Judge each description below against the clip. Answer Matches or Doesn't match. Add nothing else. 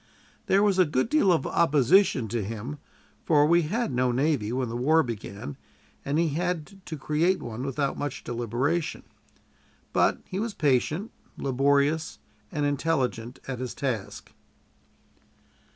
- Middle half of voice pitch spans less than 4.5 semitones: Doesn't match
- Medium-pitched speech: Matches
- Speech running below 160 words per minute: Matches